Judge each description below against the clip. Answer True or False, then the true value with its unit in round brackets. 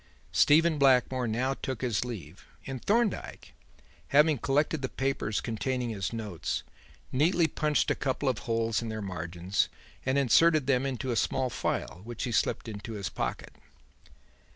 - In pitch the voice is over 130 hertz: False (125 Hz)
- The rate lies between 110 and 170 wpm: True (150 wpm)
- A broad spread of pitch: False (3.9 semitones)